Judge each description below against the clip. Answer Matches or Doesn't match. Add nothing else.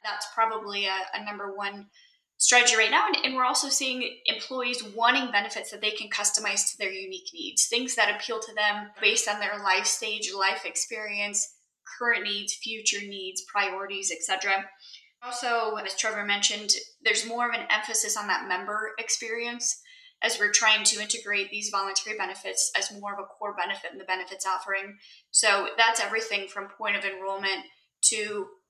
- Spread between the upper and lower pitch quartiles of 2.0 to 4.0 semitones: Matches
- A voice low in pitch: Doesn't match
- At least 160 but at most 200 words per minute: Matches